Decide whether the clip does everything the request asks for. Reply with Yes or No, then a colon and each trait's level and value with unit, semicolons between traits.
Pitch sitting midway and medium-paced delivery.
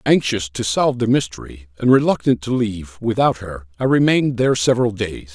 No: low, 110 Hz; average, 180 wpm